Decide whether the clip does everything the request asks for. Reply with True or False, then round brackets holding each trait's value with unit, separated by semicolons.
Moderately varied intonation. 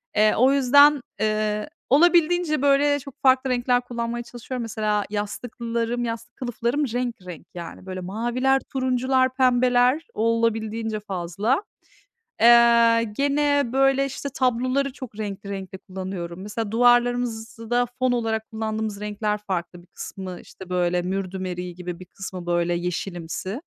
True (4.4 semitones)